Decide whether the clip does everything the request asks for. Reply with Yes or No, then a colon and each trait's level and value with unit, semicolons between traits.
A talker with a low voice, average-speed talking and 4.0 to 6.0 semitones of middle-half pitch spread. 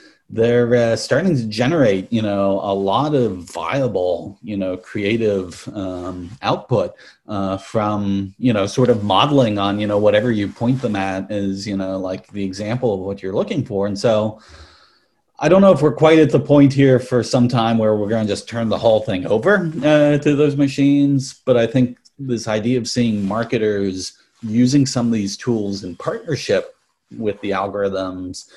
Yes: low, 110 Hz; average, 185 wpm; average, 4.5 semitones